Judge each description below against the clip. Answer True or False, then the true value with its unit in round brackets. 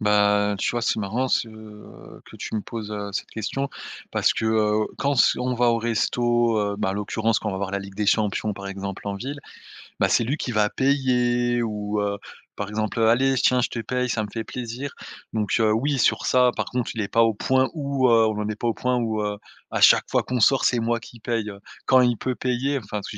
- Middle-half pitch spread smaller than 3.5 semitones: True (2.9 semitones)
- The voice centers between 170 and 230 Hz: False (115 Hz)